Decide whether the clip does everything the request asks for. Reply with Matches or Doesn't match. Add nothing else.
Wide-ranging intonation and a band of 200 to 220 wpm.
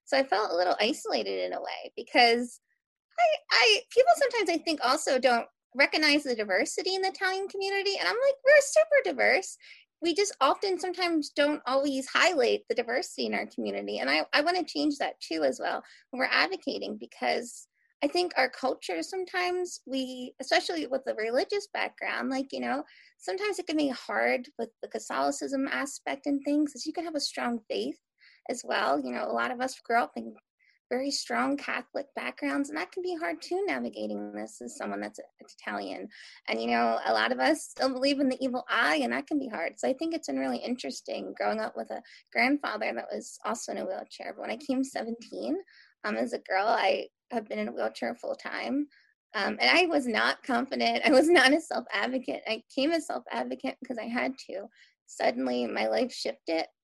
Matches